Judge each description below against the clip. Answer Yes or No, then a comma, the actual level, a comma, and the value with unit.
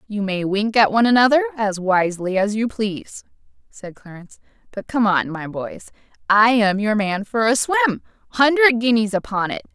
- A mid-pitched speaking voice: No, high, 220 Hz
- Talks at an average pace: Yes, average, 165 wpm